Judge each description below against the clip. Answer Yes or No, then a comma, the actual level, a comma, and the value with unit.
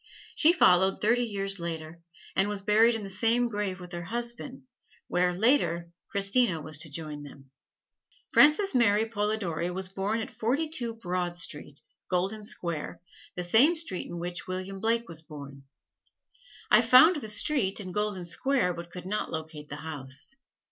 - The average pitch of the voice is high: Yes, high, 195 Hz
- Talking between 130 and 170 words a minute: Yes, average, 160 wpm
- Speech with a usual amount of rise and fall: Yes, average, 4.9 semitones